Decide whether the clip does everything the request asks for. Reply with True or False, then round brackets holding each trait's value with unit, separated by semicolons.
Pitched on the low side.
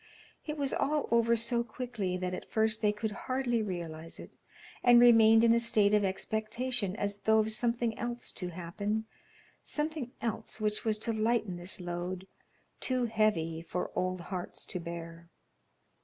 False (215 Hz)